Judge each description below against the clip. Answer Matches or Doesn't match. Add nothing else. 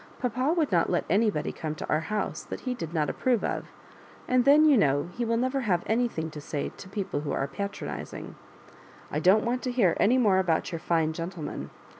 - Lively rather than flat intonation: Matches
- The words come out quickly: Matches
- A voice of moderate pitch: Doesn't match